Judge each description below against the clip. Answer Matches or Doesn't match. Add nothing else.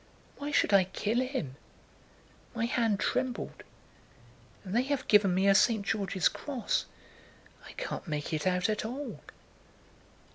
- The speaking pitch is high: Matches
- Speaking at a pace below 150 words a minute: Matches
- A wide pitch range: Doesn't match